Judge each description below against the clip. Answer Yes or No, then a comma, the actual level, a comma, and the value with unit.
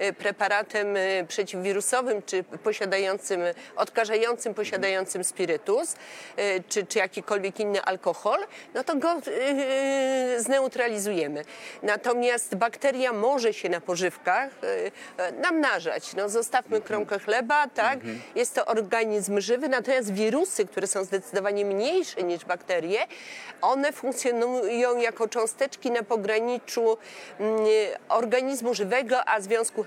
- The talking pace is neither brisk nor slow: No, slow, 100 wpm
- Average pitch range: Yes, average, 4.0 semitones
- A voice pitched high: Yes, high, 220 Hz